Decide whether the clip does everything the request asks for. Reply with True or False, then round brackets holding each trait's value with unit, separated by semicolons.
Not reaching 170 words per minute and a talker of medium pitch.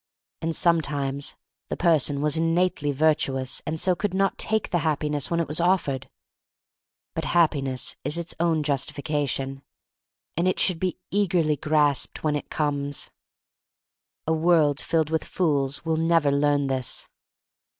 True (150 wpm; 155 Hz)